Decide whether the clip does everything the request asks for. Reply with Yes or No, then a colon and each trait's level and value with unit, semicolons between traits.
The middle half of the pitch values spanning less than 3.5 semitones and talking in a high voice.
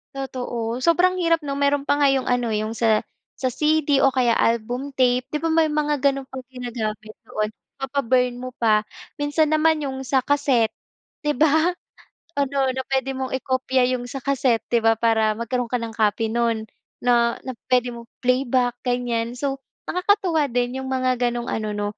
Yes: average, 3.0 semitones; very high, 255 Hz